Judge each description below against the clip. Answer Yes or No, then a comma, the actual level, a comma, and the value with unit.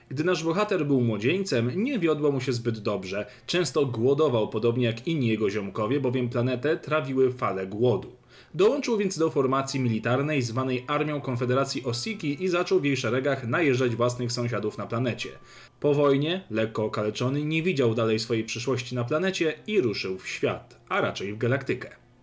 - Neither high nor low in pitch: No, low, 130 Hz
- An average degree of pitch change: Yes, average, 4.1 semitones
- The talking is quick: Yes, fast, 165 wpm